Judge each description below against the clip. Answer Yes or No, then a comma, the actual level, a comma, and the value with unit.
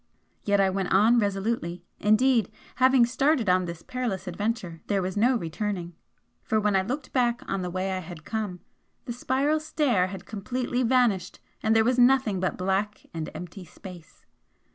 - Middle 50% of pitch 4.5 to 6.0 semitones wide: Yes, average, 4.8 semitones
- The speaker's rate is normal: Yes, average, 170 wpm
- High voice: Yes, high, 205 Hz